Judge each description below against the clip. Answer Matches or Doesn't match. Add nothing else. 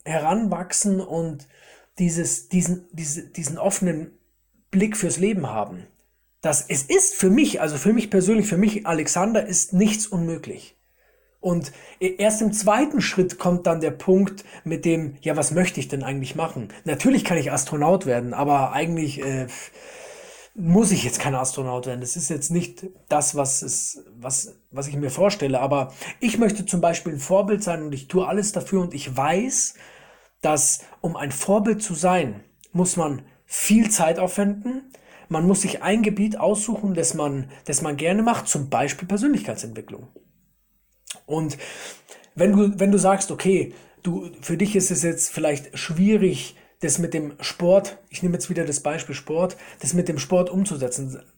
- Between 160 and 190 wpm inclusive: Matches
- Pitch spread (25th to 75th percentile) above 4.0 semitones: Matches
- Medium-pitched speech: Matches